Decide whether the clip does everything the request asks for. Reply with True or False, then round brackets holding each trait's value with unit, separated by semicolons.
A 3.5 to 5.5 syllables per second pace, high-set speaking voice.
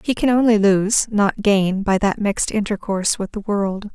True (4.7 syllables/s; 205 Hz)